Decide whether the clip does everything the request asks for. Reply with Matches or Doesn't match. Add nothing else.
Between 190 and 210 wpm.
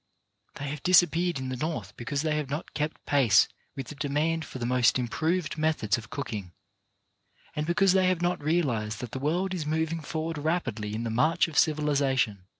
Matches